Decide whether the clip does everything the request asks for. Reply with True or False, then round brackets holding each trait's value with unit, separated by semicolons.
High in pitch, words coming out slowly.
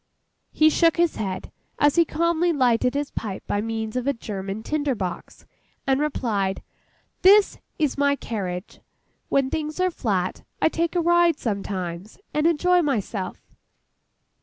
False (275 Hz; 145 wpm)